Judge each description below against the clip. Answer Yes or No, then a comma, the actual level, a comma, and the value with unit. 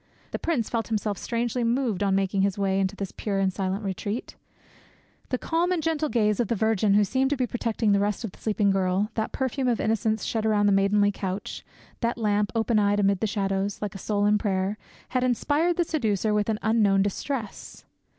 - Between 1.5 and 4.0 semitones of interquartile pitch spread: Yes, average, 2.8 semitones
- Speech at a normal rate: No, fast, 210 wpm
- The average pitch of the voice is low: No, high, 210 Hz